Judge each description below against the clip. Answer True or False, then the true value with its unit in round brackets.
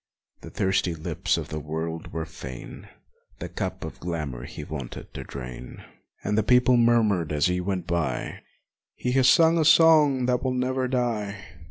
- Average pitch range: False (7.8 semitones)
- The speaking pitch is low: True (100 Hz)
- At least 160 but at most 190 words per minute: True (170 wpm)